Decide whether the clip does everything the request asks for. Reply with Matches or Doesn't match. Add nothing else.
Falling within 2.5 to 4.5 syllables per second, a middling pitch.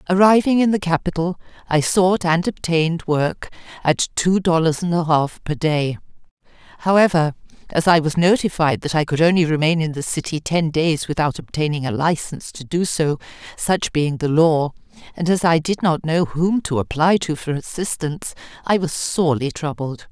Doesn't match